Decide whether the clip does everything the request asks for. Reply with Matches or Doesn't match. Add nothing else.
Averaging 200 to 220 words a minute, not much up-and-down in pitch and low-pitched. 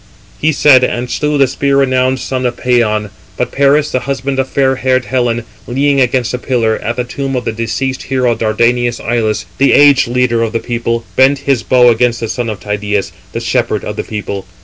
Matches